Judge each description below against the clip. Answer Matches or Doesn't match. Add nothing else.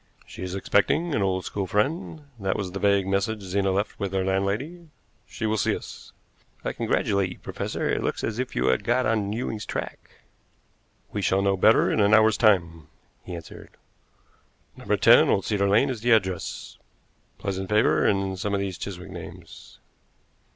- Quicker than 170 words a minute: Matches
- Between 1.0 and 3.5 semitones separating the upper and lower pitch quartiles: Matches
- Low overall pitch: Matches